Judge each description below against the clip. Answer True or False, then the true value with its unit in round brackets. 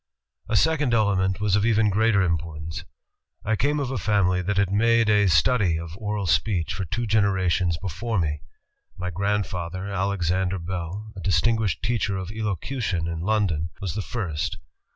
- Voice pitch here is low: True (100 Hz)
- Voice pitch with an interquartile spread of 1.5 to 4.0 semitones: True (3.5 semitones)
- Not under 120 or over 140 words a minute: False (160 wpm)